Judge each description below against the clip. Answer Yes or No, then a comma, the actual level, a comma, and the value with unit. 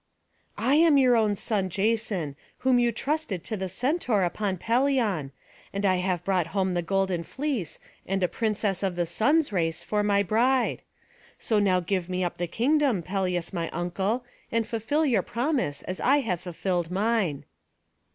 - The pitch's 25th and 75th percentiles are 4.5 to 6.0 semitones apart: Yes, average, 4.9 semitones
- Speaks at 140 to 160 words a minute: No, average, 170 wpm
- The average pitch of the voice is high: Yes, high, 200 Hz